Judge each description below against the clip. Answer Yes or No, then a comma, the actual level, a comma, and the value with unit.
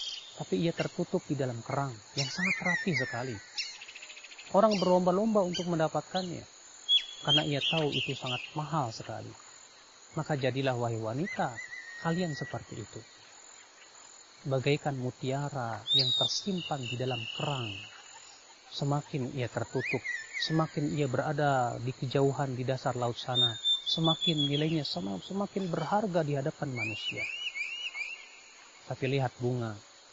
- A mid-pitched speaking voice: Yes, medium, 145 Hz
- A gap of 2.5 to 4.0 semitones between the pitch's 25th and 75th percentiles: No, average, 4.7 semitones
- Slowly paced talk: No, average, 115 wpm